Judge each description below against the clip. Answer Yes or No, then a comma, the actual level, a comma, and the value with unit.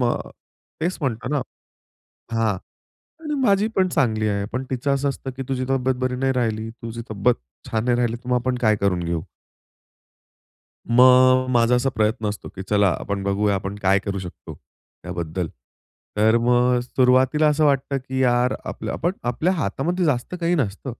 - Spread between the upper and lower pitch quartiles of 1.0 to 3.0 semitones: No, average, 3.7 semitones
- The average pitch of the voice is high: No, low, 125 Hz